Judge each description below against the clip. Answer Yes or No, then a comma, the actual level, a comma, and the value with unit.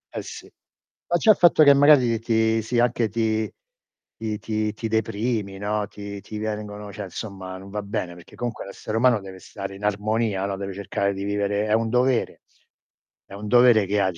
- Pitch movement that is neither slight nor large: No, narrow, 2.3 semitones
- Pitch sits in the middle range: No, low, 105 Hz